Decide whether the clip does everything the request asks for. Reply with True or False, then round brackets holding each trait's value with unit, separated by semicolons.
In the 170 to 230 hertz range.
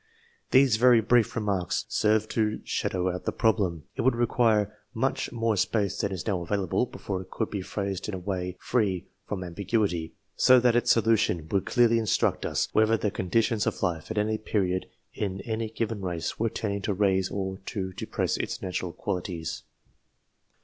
False (105 Hz)